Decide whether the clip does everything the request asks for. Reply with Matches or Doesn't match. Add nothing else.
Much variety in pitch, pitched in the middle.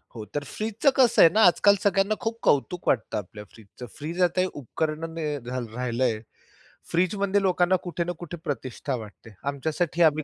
Matches